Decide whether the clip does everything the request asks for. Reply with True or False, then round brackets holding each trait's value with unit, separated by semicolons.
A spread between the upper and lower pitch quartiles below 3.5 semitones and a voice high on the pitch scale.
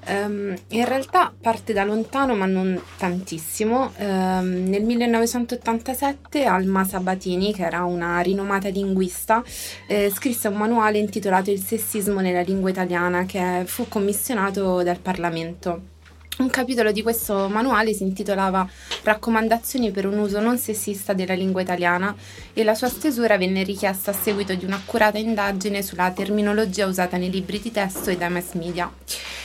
True (3.0 semitones; 200 Hz)